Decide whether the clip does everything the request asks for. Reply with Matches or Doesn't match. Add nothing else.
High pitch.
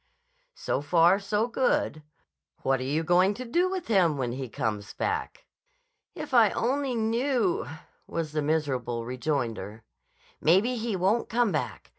Doesn't match